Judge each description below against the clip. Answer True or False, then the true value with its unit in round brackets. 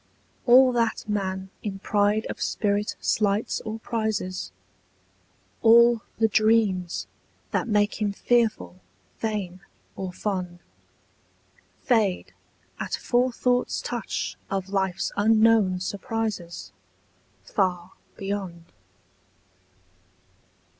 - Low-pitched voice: False (205 Hz)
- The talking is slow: True (85 wpm)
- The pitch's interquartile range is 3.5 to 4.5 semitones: False (3.0 semitones)